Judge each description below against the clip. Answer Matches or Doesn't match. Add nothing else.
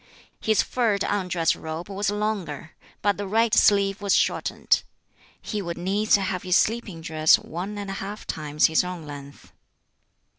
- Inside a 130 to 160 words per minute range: Matches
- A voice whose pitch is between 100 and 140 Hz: Doesn't match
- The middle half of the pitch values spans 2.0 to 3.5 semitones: Doesn't match